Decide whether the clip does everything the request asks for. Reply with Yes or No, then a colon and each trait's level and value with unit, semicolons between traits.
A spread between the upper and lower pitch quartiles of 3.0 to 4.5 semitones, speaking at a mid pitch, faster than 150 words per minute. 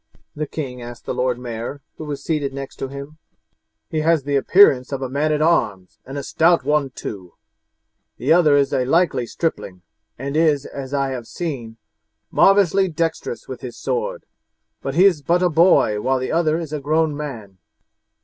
Yes: average, 3.9 semitones; medium, 145 Hz; average, 185 wpm